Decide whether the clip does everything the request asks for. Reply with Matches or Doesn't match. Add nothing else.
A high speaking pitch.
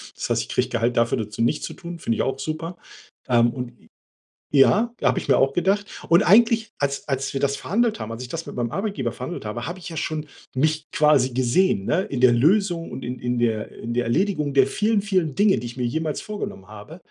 Doesn't match